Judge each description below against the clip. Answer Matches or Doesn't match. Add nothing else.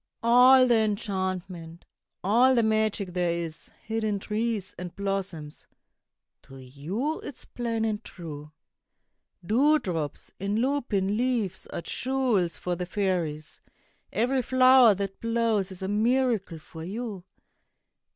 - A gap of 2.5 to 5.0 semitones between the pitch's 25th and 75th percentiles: Matches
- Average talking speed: Doesn't match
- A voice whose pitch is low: Doesn't match